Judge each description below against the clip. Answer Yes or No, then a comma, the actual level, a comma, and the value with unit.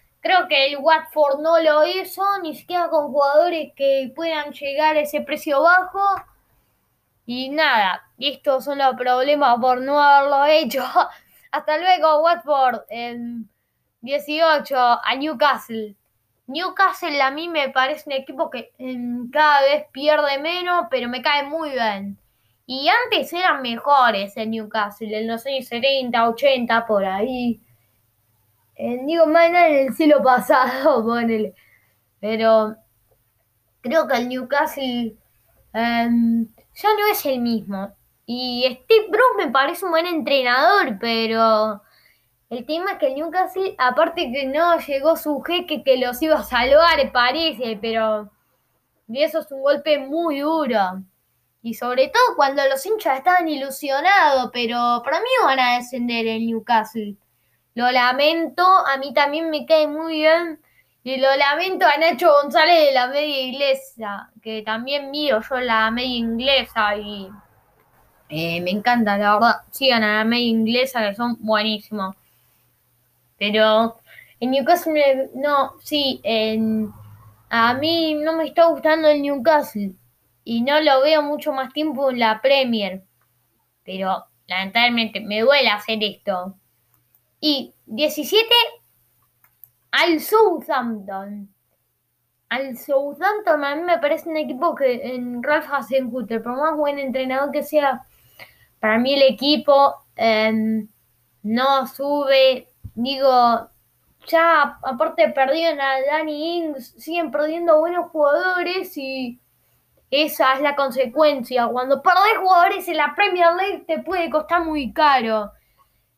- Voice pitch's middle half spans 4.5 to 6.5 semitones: Yes, average, 5.2 semitones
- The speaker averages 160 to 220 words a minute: No, average, 135 wpm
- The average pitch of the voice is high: Yes, very high, 270 Hz